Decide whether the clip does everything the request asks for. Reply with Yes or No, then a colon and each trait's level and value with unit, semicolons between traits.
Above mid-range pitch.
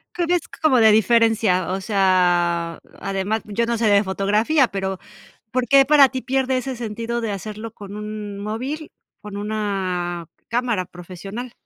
Yes: high, 215 Hz